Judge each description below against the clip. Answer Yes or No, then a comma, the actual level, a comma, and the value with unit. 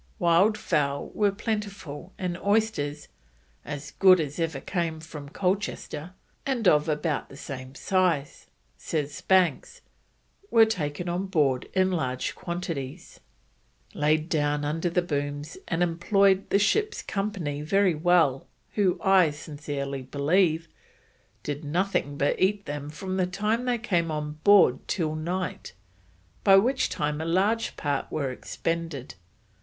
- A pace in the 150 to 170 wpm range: No, slow, 135 wpm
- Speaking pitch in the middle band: Yes, medium, 165 Hz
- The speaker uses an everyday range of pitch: Yes, average, 4.7 semitones